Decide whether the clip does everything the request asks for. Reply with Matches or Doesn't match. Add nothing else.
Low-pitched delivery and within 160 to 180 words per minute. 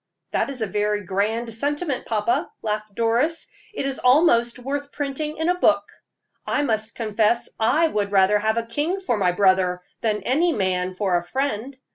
Doesn't match